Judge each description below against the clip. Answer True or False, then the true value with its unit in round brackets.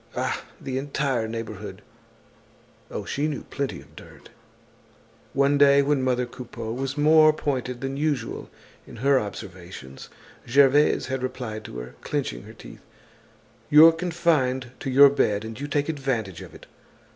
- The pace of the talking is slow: False (145 wpm)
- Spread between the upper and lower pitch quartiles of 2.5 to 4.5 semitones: True (4.1 semitones)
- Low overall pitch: True (130 Hz)